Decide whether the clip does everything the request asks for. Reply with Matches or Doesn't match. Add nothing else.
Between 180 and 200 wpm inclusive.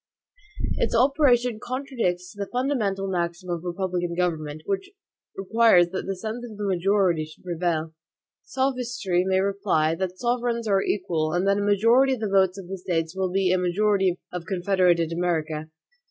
Doesn't match